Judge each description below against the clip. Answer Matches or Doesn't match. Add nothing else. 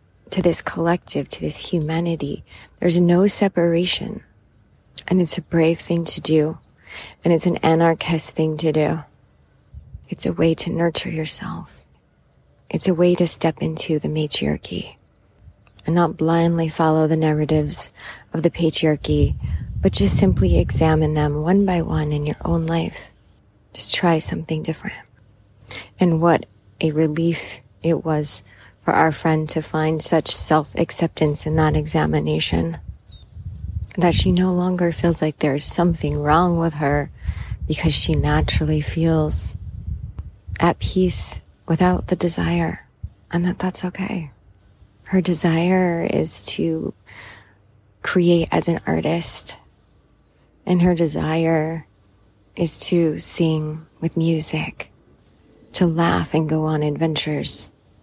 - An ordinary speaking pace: Doesn't match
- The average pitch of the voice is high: Doesn't match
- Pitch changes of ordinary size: Doesn't match